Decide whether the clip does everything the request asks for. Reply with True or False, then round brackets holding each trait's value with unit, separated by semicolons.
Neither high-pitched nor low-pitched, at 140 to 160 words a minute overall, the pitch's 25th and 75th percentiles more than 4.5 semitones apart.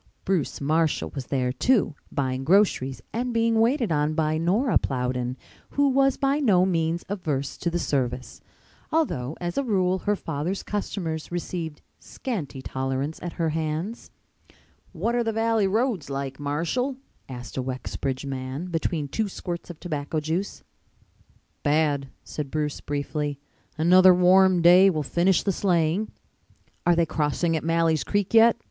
True (165 Hz; 150 wpm; 5.3 semitones)